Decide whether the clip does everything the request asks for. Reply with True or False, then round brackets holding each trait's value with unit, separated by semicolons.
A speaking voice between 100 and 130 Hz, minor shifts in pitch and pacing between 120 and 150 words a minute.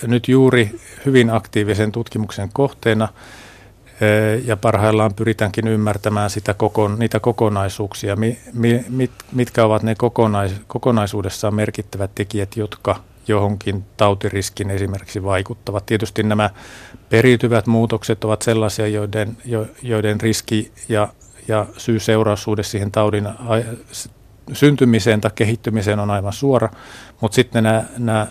False (110 Hz; 1.8 semitones; 110 wpm)